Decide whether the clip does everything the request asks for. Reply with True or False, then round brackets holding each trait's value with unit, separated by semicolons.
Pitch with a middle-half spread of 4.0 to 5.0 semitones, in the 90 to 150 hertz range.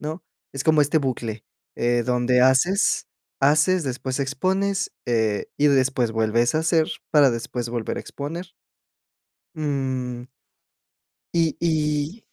True (4.3 semitones; 135 Hz)